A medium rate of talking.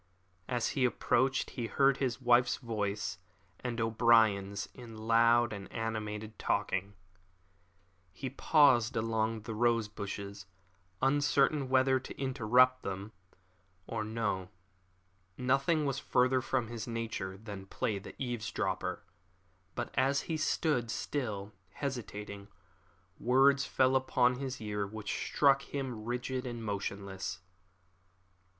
No: slow, 115 wpm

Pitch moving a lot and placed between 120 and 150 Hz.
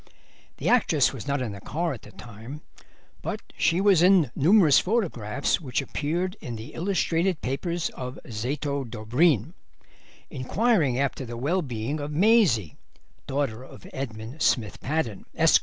Yes: wide, 6.2 semitones; medium, 140 Hz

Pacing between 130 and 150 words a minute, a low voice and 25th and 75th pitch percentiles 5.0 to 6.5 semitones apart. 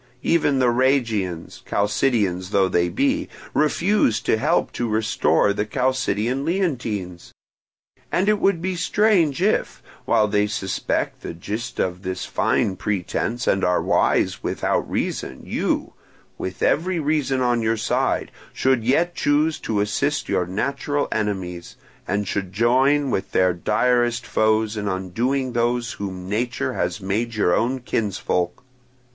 Yes: average, 140 wpm; low, 115 Hz; wide, 5.6 semitones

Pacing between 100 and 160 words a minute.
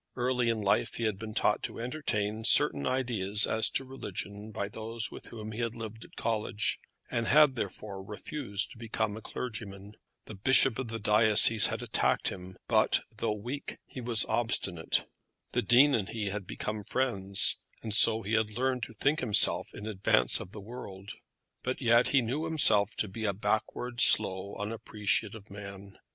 No: average, 175 wpm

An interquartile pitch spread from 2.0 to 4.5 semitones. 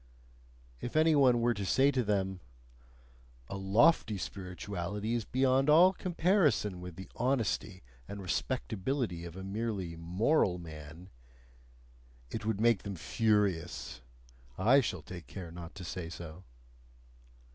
No: average, 5.3 semitones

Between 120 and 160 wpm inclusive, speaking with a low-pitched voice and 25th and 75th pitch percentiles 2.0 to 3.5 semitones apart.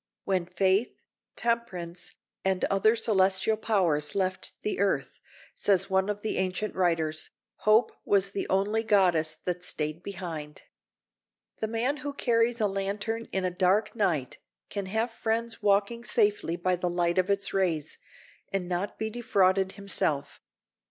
No: average, 145 wpm; high, 195 Hz; average, 3.2 semitones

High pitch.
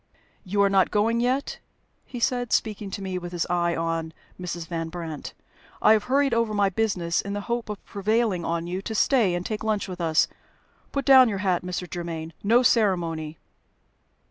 Yes: high, 195 Hz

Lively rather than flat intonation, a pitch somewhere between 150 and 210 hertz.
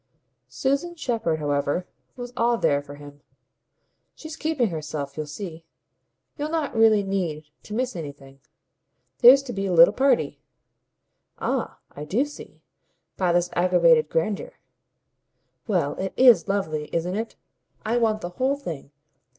Yes: wide, 7.8 semitones; high, 190 Hz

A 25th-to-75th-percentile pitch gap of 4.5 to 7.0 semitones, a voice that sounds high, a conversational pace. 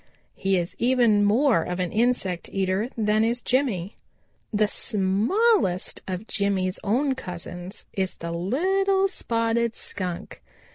No: average, 4.8 semitones; high, 210 Hz; slow, 125 wpm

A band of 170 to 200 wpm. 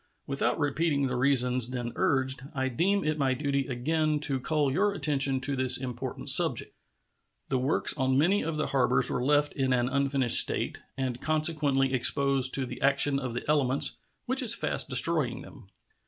Yes: average, 175 wpm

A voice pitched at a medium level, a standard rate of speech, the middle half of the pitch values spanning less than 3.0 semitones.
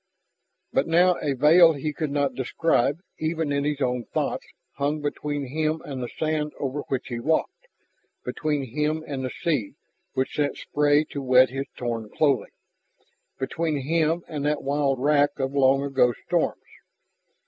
Yes: medium, 145 Hz; average, 160 wpm; narrow, 2.5 semitones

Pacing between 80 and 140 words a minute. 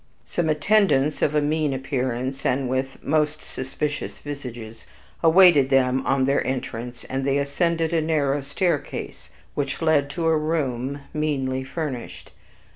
Yes: slow, 135 wpm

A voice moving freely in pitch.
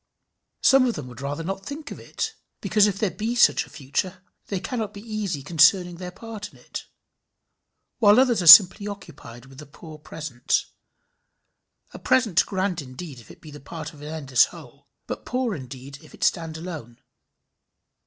Yes: wide, 6.2 semitones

